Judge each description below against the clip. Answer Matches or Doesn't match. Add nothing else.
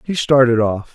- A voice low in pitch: Matches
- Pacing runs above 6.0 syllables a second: Doesn't match